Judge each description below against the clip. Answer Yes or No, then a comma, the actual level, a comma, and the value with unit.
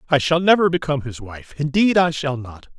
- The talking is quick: No, average, 195 wpm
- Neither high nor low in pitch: Yes, medium, 145 Hz